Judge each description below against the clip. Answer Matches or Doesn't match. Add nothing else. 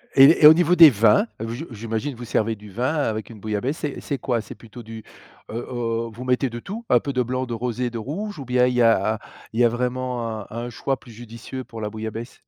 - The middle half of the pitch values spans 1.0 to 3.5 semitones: Matches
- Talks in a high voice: Doesn't match